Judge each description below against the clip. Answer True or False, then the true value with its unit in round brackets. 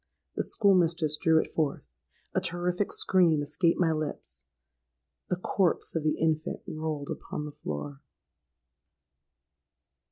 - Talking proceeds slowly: True (115 wpm)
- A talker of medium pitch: True (155 Hz)